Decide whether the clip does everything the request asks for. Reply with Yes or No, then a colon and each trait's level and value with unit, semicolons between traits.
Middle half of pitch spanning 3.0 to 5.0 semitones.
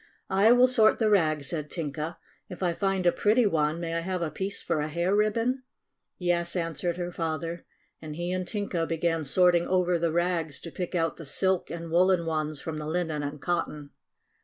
No: narrow, 2.5 semitones